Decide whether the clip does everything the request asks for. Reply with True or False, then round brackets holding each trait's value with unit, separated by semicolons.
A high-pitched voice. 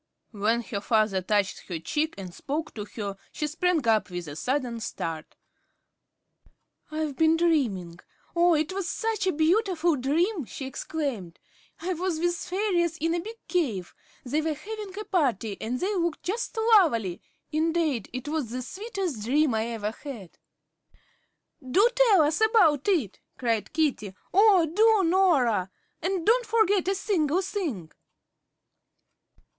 True (310 Hz)